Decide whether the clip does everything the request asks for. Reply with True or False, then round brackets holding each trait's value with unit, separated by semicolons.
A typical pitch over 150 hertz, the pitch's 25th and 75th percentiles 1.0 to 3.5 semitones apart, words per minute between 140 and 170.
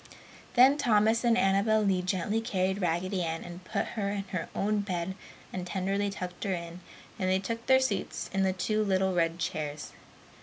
False (190 Hz; 2.8 semitones; 185 wpm)